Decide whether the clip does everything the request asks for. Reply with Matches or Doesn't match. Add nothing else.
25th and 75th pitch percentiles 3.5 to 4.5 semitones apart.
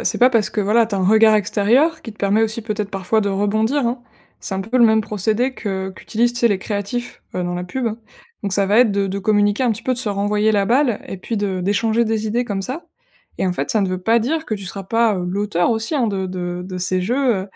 Doesn't match